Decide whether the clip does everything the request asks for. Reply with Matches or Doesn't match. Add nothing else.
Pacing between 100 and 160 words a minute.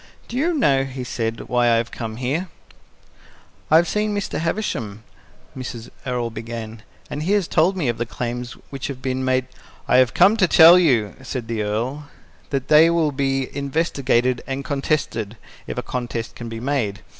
Doesn't match